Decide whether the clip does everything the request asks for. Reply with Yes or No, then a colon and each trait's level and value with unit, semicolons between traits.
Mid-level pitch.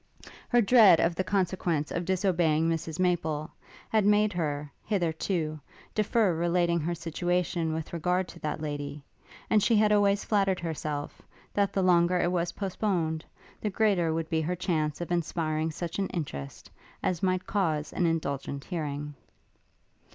Yes: medium, 170 Hz